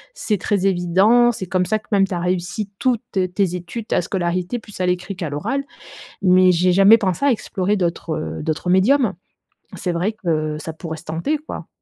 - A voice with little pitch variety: No, average, 3.3 semitones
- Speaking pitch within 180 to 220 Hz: Yes, medium, 185 Hz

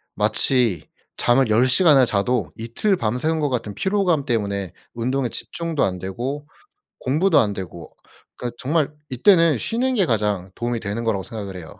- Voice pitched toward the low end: Yes, low, 120 Hz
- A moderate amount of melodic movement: No, wide, 6.2 semitones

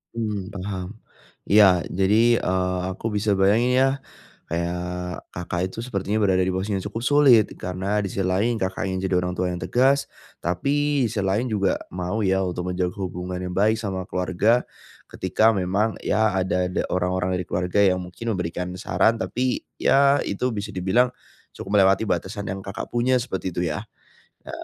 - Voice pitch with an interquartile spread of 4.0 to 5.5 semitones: No, average, 3.2 semitones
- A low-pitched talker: Yes, very low, 95 Hz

